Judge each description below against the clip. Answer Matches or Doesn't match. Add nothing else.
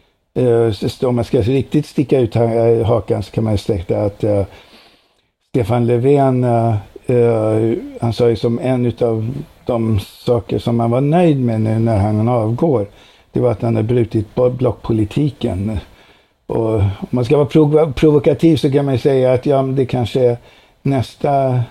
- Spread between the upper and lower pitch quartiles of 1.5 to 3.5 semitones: Matches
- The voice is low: Matches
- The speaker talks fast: Doesn't match